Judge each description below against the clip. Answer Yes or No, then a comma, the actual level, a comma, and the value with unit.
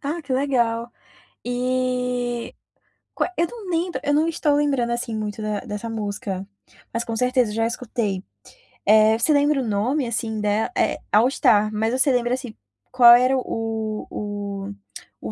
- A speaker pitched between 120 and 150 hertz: No, high, 240 Hz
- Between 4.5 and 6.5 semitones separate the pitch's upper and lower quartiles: No, average, 3.4 semitones